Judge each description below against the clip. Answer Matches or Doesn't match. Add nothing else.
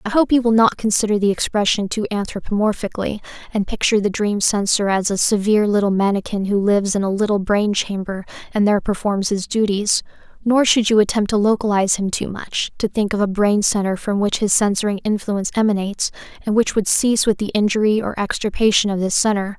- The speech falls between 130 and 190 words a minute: Doesn't match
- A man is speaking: Doesn't match